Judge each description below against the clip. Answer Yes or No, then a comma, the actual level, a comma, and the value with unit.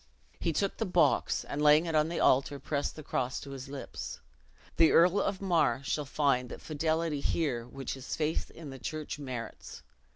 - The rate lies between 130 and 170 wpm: No, average, 190 wpm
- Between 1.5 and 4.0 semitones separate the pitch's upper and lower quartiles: Yes, average, 3.2 semitones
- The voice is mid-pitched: Yes, medium, 150 Hz